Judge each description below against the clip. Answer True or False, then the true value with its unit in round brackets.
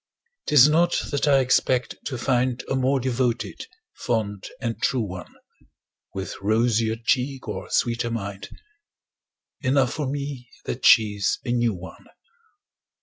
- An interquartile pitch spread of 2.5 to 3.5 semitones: True (3.0 semitones)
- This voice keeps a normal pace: False (130 wpm)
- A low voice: True (120 Hz)